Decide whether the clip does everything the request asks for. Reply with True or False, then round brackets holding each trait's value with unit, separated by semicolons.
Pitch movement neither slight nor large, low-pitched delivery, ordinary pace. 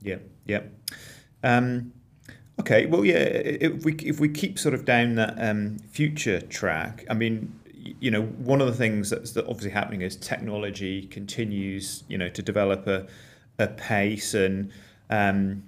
True (3.7 semitones; 110 Hz; 155 wpm)